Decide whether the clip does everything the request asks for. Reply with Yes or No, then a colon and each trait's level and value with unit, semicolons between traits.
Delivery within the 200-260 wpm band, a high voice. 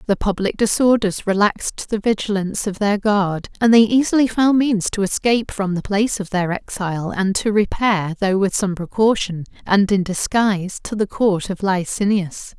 No: average, 175 wpm; high, 200 Hz